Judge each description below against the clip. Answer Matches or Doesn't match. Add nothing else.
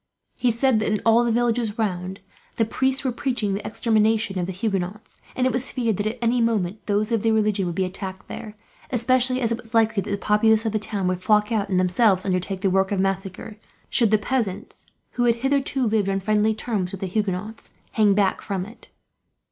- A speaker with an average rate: Doesn't match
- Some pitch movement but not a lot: Matches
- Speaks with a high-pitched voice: Matches